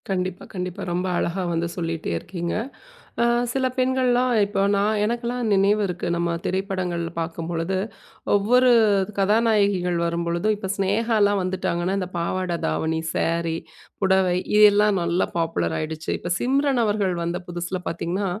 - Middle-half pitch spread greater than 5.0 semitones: No, average, 3.4 semitones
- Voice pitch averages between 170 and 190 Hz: Yes, medium, 185 Hz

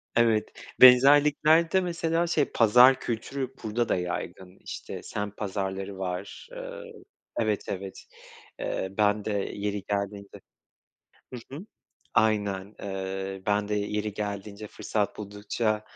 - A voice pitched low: Yes, low, 105 Hz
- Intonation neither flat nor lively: Yes, average, 3.8 semitones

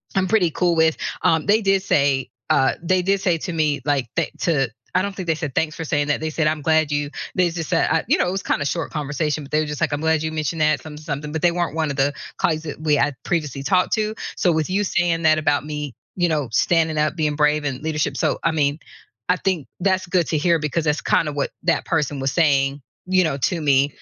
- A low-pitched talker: No, medium, 155 Hz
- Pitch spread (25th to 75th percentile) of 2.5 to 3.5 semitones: Yes, average, 2.8 semitones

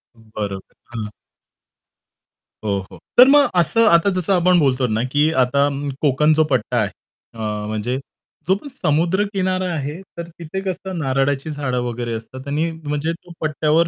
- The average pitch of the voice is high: No, medium, 150 Hz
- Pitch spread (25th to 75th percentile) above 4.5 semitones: Yes, average, 5.3 semitones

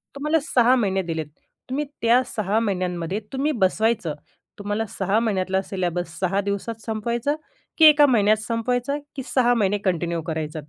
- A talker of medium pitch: No, high, 210 Hz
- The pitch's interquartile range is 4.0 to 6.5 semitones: Yes, average, 4.7 semitones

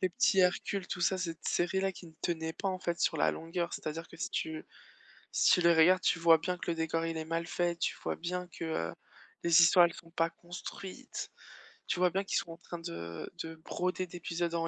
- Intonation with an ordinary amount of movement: No, narrow, 1.7 semitones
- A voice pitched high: No, medium, 170 Hz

